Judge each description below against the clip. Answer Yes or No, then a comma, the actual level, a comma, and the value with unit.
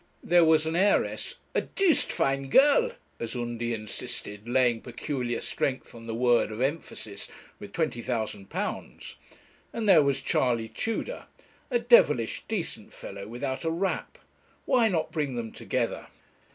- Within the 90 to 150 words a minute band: Yes, average, 140 wpm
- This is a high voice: No, low, 130 Hz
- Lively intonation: Yes, wide, 6.4 semitones